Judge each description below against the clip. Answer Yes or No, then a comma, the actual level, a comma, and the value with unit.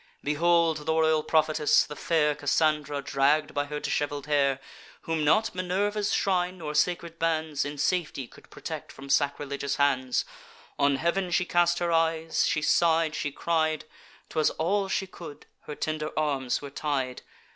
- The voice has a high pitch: No, medium, 155 Hz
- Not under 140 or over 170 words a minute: Yes, average, 155 wpm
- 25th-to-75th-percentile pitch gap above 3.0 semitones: No, average, 2.7 semitones